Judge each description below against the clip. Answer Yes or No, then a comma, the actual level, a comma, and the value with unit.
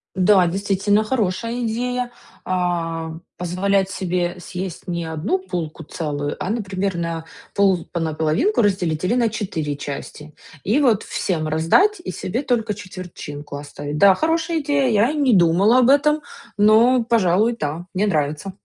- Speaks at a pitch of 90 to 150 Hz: No, high, 190 Hz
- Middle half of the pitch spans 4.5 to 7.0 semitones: Yes, wide, 5.6 semitones